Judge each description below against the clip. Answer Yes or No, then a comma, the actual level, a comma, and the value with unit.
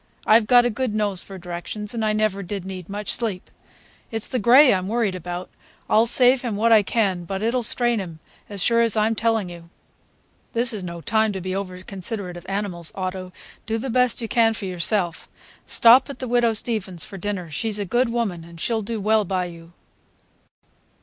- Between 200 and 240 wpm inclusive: Yes, fast, 205 wpm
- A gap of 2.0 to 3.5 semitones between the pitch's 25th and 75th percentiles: No, average, 3.9 semitones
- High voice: Yes, high, 210 Hz